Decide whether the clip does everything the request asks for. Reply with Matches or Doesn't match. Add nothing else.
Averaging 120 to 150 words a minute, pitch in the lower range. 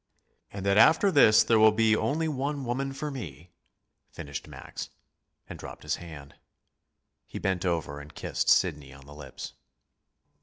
Doesn't match